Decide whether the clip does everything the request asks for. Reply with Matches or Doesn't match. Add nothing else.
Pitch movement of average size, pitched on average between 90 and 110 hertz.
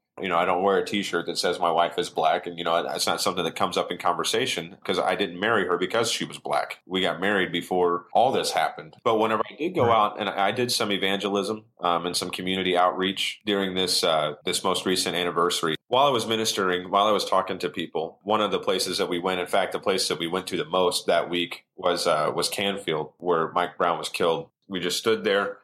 Doesn't match